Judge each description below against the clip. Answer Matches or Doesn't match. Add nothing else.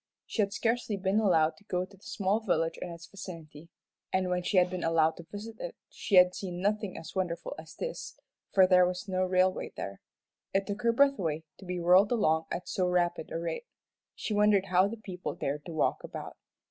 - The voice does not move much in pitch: Doesn't match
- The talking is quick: Matches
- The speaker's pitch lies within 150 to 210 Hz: Matches